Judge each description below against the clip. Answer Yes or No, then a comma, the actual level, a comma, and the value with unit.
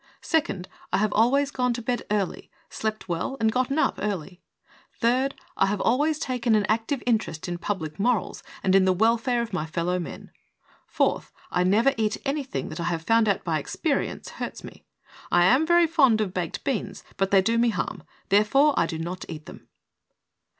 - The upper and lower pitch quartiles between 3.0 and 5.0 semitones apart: No, wide, 5.4 semitones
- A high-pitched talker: Yes, high, 220 Hz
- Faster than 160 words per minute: Yes, average, 190 wpm